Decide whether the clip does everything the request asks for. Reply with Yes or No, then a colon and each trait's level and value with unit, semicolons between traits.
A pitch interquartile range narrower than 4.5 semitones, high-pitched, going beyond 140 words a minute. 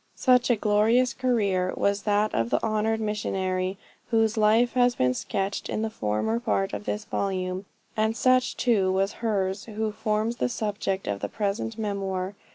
Yes: average, 2.9 semitones; high, 210 Hz; average, 165 wpm